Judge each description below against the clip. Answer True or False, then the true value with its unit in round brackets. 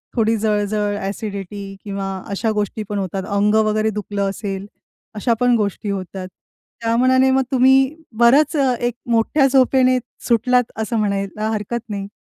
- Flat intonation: False (3.6 semitones)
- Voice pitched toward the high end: True (215 Hz)